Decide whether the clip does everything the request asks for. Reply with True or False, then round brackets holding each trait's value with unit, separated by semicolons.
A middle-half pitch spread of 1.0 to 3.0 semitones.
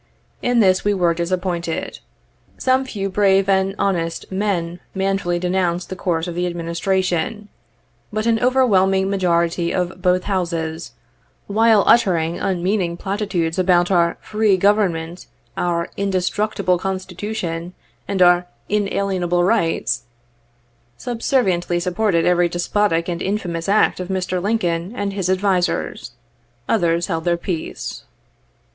True (2.5 semitones)